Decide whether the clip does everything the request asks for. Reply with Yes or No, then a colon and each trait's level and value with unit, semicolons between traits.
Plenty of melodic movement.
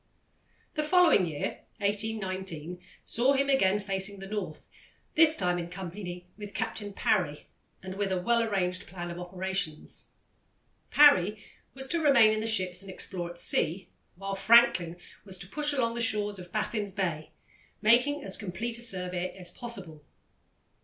No: average, 4.0 semitones